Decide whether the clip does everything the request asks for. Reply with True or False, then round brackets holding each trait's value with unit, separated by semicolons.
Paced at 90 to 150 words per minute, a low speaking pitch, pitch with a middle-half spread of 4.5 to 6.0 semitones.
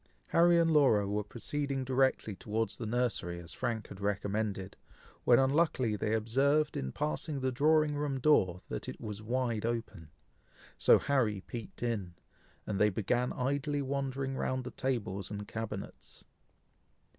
True (145 wpm; 120 Hz; 4.8 semitones)